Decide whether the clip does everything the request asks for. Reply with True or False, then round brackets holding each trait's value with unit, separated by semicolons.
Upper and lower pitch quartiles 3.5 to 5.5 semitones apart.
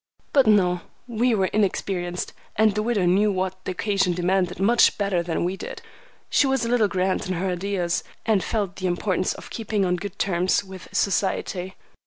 False (2.7 semitones)